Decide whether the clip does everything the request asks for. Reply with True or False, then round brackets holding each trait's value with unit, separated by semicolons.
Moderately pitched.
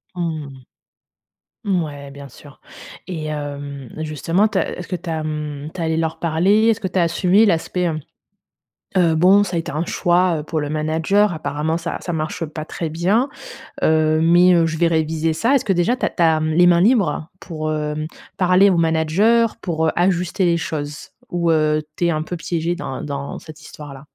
True (165 Hz)